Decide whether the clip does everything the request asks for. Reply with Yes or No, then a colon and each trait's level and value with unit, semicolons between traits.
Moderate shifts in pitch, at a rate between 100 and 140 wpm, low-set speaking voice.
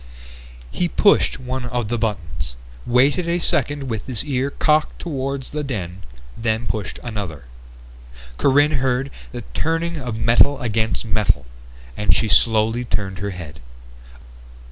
Yes: average, 4.9 semitones; slow, 135 wpm; low, 120 Hz